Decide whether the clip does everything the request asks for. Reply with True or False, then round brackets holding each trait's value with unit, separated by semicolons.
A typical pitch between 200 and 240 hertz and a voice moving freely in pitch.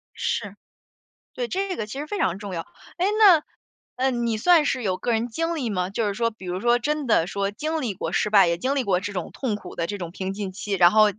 True (215 Hz; 6.2 semitones)